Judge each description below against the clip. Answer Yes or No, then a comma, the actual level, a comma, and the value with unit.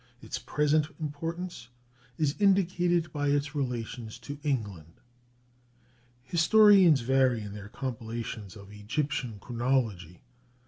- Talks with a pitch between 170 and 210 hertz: No, low, 135 Hz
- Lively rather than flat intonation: Yes, wide, 5.7 semitones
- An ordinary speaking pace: No, slow, 100 wpm